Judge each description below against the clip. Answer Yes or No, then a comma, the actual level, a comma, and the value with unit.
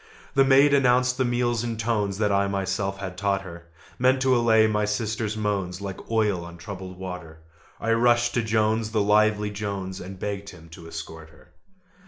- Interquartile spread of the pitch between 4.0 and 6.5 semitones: No, average, 3.3 semitones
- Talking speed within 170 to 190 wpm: Yes, average, 185 wpm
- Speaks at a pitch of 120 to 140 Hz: No, low, 105 Hz